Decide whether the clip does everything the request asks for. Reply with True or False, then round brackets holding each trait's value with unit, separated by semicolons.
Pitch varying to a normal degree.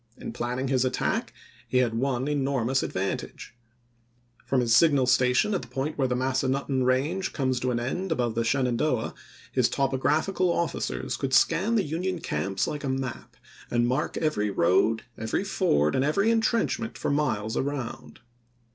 True (3.8 semitones)